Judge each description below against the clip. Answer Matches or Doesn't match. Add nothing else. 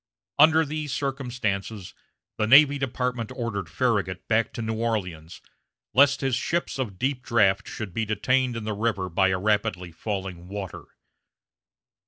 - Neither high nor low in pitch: Doesn't match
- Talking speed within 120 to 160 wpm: Matches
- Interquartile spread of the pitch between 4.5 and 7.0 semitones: Matches